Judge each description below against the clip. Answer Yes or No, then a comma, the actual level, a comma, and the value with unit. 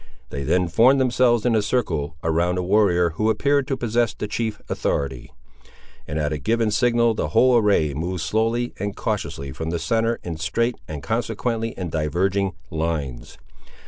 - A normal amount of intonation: No, wide, 6.4 semitones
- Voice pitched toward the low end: Yes, low, 100 Hz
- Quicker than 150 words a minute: Yes, average, 170 wpm